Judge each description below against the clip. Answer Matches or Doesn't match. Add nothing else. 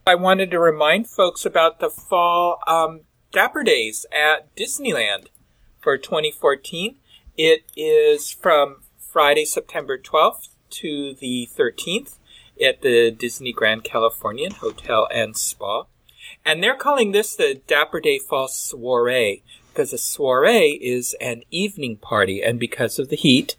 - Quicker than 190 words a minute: Doesn't match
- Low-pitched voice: Doesn't match